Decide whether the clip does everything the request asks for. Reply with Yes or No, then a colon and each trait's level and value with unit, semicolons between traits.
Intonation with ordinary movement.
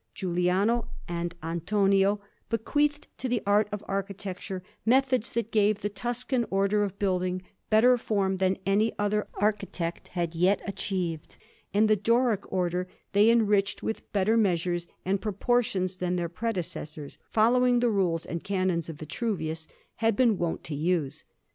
Yes: average, 3.6 semitones